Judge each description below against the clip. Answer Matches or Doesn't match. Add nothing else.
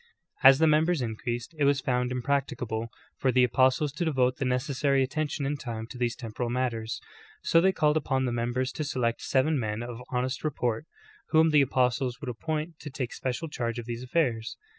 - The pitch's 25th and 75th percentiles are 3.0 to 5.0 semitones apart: Matches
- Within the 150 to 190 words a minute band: Doesn't match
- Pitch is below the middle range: Matches